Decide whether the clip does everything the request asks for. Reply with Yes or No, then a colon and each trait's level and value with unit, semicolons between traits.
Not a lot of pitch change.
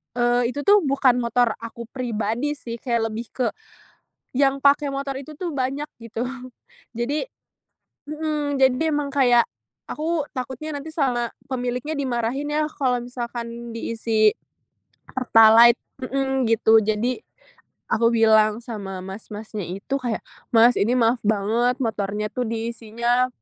No: average, 3.3 semitones